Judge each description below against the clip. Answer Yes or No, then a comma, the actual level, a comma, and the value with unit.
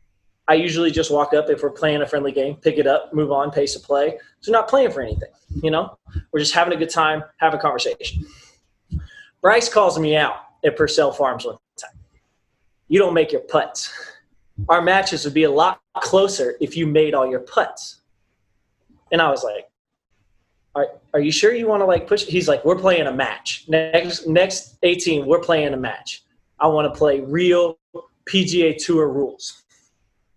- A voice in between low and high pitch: Yes, medium, 160 Hz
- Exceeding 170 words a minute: Yes, average, 190 wpm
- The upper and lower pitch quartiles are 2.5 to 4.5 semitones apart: Yes, average, 3.9 semitones